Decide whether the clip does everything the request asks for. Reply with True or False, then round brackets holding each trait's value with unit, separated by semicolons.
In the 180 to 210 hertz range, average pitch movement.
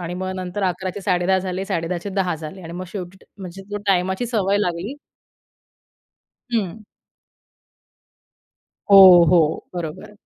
False (185 Hz; 1.8 semitones)